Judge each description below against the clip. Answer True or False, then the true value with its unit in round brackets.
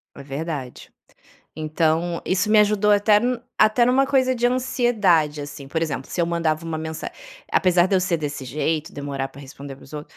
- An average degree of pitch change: False (6.0 semitones)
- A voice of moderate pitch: True (165 Hz)